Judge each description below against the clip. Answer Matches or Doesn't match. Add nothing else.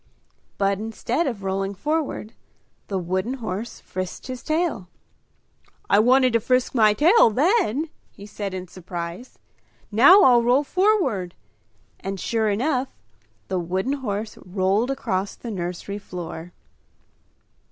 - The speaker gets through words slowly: Matches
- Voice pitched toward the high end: Matches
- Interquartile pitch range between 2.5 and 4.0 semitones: Doesn't match